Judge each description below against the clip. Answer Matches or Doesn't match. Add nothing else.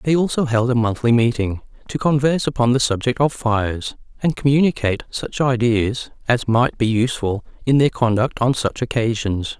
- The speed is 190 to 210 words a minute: Doesn't match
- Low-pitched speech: Matches